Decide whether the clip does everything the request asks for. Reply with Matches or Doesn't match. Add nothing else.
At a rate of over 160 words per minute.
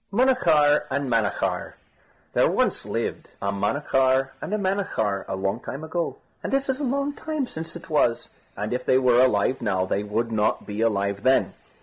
Matches